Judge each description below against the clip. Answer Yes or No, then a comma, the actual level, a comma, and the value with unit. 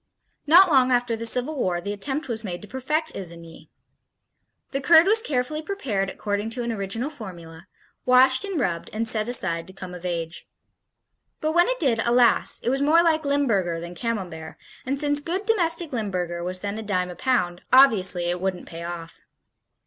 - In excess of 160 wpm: Yes, average, 185 wpm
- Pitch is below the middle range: No, high, 230 Hz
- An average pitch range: No, wide, 7.8 semitones